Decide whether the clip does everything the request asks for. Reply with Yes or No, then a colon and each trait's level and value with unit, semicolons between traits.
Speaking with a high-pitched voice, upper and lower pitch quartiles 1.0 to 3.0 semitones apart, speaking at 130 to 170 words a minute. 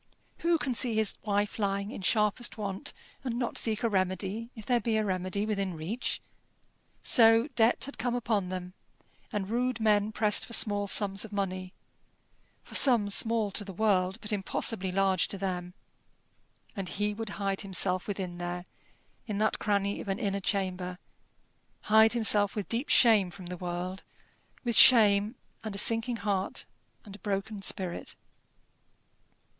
Yes: high, 205 Hz; average, 2.7 semitones; average, 160 wpm